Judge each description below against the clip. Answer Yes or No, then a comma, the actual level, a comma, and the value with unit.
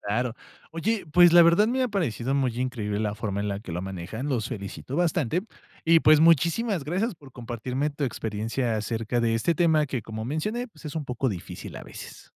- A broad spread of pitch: Yes, wide, 7.0 semitones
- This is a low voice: Yes, low, 130 Hz